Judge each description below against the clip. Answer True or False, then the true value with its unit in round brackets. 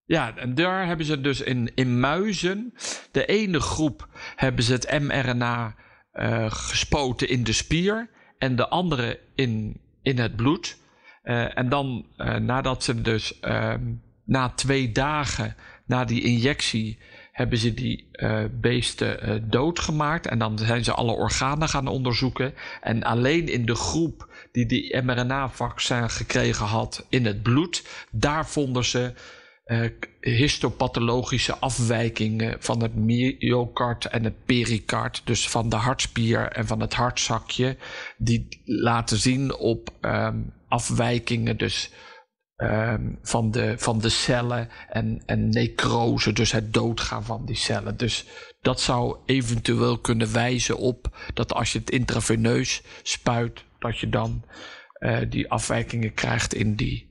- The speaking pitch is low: True (120 Hz)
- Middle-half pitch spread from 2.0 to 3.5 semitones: True (2.4 semitones)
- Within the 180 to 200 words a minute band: False (140 wpm)